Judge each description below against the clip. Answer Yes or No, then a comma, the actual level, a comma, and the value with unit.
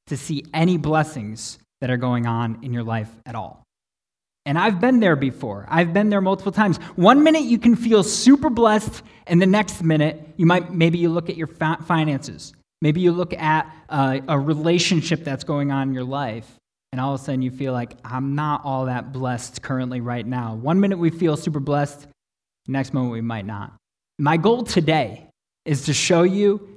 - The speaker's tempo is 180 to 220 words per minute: Yes, average, 200 wpm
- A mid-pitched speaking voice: Yes, medium, 150 Hz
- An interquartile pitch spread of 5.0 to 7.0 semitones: Yes, wide, 5.4 semitones